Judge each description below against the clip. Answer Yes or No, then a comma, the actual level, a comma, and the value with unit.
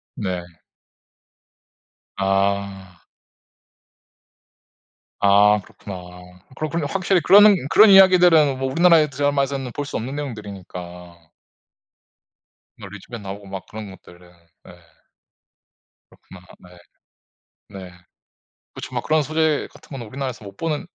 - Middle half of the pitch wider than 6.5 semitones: Yes, wide, 7.5 semitones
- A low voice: Yes, low, 110 Hz